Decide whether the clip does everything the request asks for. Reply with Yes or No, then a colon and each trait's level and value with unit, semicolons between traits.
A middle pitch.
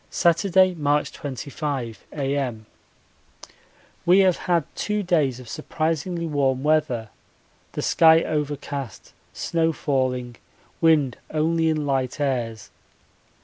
Yes: medium, 150 Hz